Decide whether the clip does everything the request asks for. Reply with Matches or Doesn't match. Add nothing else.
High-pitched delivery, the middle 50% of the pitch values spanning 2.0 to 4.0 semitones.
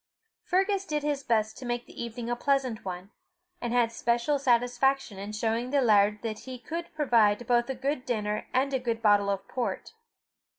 Matches